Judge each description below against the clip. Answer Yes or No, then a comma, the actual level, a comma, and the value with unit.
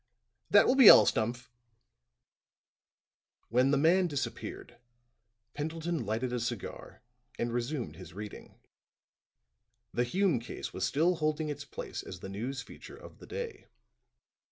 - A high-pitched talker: No, low, 135 Hz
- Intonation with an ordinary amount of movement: No, wide, 5.7 semitones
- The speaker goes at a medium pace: No, slow, 130 wpm